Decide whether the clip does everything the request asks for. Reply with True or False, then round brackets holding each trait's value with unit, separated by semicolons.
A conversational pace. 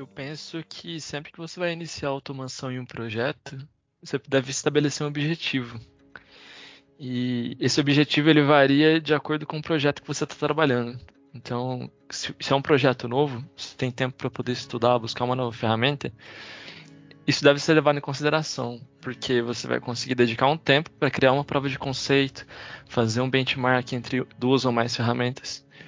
True (175 wpm)